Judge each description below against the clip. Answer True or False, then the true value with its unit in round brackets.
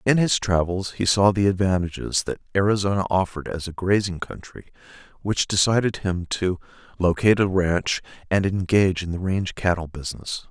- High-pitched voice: False (95 Hz)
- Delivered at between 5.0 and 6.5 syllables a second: True (5.5 syllables/s)